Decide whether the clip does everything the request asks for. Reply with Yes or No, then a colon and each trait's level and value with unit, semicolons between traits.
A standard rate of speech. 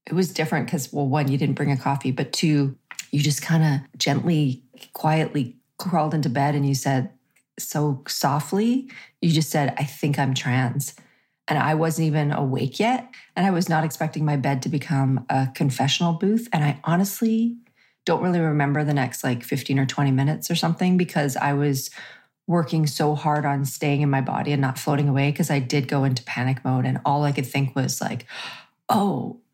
Yes: average, 195 wpm